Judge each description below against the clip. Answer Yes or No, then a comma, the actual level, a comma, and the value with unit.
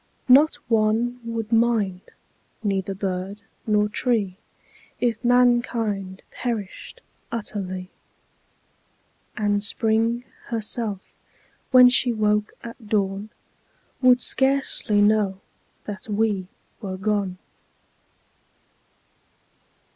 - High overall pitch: Yes, high, 215 Hz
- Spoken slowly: Yes, slow, 80 wpm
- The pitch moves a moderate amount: Yes, average, 3.0 semitones